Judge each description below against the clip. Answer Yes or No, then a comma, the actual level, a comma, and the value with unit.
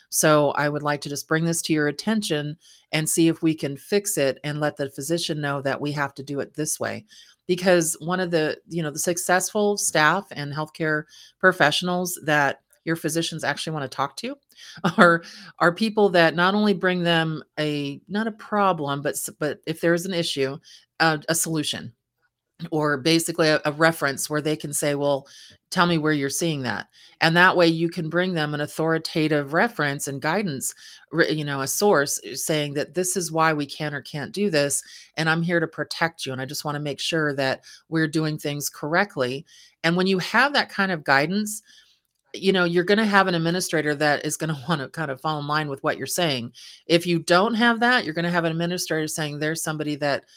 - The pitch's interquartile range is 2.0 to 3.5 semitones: Yes, average, 3.1 semitones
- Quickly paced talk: Yes, fast, 210 wpm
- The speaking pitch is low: No, medium, 160 Hz